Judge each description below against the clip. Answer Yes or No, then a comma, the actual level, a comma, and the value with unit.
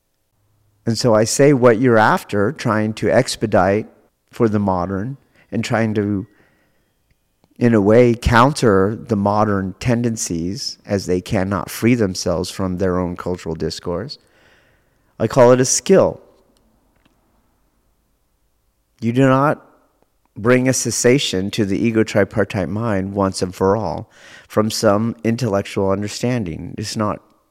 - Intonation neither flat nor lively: Yes, average, 3.6 semitones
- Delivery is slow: Yes, slow, 130 wpm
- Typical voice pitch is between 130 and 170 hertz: No, low, 105 Hz